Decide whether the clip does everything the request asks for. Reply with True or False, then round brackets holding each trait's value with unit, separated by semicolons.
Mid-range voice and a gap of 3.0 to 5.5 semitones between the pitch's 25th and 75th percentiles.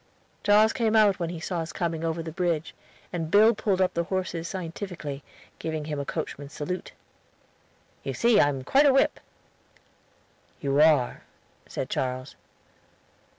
True (170 Hz; 4.4 semitones)